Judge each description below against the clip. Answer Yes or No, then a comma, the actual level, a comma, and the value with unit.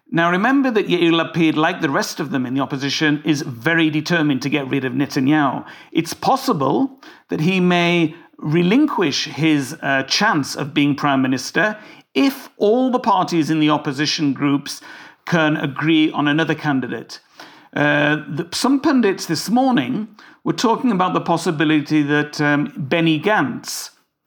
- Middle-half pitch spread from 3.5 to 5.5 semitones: Yes, average, 3.8 semitones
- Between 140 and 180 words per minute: Yes, average, 155 wpm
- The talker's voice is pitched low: No, medium, 160 Hz